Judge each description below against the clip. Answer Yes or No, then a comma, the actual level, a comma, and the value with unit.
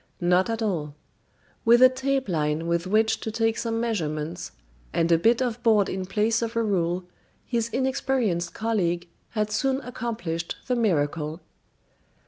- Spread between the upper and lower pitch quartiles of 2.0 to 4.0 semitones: No, wide, 5.4 semitones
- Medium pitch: No, high, 215 Hz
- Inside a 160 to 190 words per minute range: No, average, 150 wpm